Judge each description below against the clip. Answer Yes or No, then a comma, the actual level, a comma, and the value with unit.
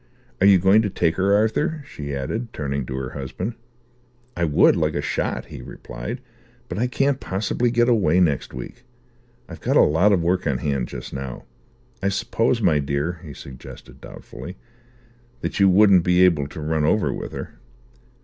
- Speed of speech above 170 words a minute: Yes, average, 180 wpm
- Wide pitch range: Yes, wide, 6.5 semitones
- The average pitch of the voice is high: No, very low, 90 Hz